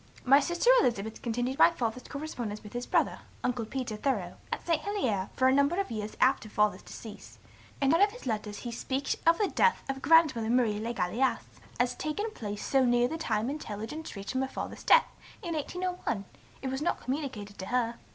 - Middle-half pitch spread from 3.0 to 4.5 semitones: No, wide, 5.6 semitones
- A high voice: Yes, very high, 255 Hz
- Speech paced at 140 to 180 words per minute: No, average, 200 wpm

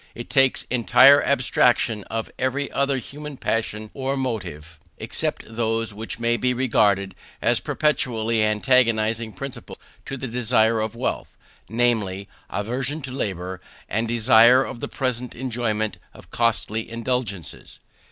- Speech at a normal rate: No, slow, 130 wpm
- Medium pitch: No, low, 115 Hz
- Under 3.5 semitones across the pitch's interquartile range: Yes, average, 2.9 semitones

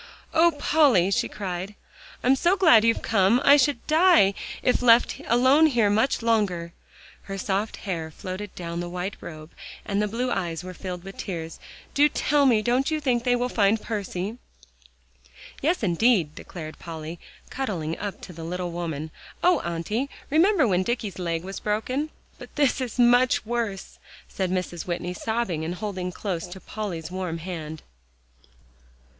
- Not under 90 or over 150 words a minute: No, average, 160 wpm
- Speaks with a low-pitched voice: No, high, 200 Hz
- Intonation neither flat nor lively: No, wide, 5.7 semitones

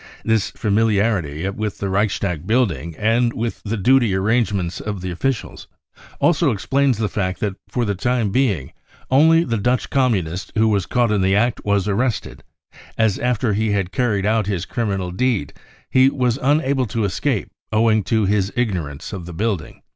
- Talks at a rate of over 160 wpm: Yes, average, 170 wpm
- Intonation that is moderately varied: Yes, average, 3.9 semitones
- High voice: No, low, 105 Hz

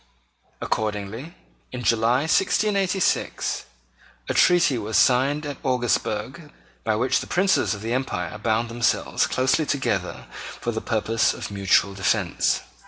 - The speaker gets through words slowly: Yes, slow, 125 wpm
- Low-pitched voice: Yes, low, 120 Hz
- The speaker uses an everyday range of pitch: Yes, average, 5.0 semitones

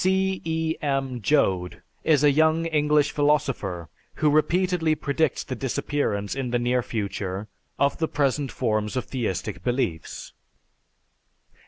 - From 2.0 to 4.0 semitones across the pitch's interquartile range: No, average, 4.8 semitones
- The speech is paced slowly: Yes, slow, 130 wpm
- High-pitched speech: No, medium, 140 Hz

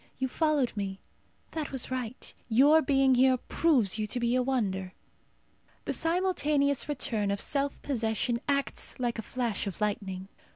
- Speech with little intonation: No, average, 4.6 semitones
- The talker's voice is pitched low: No, very high, 255 Hz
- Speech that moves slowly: No, average, 155 wpm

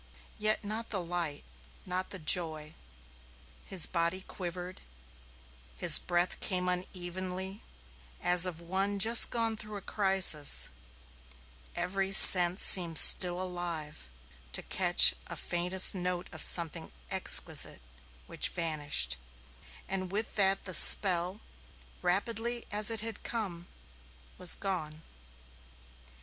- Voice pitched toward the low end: No, medium, 180 Hz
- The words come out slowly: Yes, slow, 110 wpm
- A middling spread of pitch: No, narrow, 2.2 semitones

